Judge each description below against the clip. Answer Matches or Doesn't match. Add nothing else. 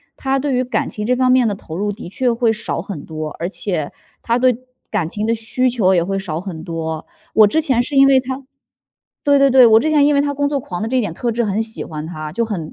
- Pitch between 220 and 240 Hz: Matches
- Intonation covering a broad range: Matches